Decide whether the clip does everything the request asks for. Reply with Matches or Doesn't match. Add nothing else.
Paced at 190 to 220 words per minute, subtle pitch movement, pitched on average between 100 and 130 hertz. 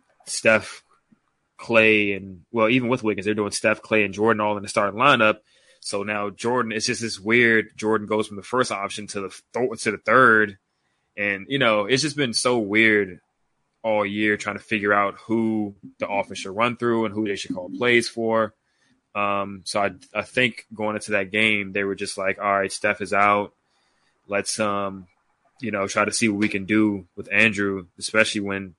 Matches